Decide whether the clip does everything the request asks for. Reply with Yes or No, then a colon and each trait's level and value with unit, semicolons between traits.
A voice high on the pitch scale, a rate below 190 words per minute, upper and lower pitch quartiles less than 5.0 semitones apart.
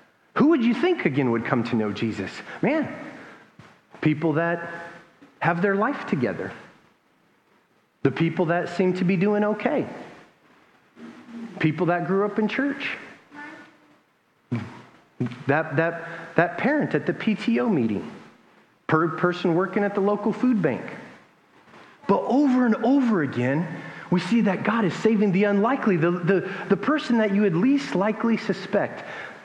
No: high, 200 Hz; average, 145 wpm; wide, 5.4 semitones